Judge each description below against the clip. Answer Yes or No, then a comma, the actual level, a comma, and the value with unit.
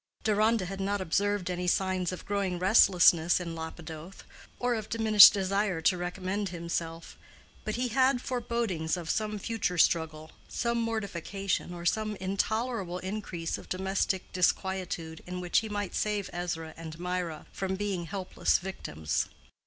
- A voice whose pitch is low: No, high, 190 Hz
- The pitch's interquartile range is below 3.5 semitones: Yes, average, 3.1 semitones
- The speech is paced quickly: No, average, 145 wpm